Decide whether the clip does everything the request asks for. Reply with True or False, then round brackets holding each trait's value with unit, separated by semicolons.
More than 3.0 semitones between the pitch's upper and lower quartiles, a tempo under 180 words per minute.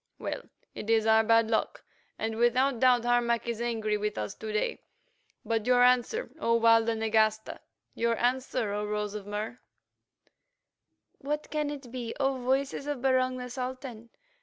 False (2.6 semitones; 160 wpm)